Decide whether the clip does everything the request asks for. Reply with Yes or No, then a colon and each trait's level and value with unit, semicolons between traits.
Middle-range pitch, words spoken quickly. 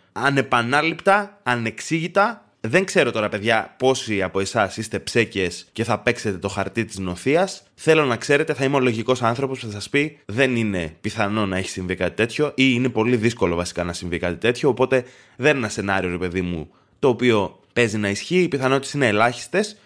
No: low, 115 Hz; fast, 195 wpm